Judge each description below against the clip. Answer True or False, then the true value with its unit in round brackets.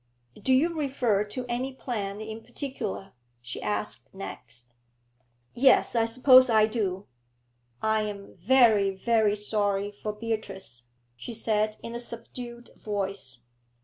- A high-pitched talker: True (215 Hz)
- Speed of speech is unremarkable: False (125 wpm)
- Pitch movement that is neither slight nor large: True (3.3 semitones)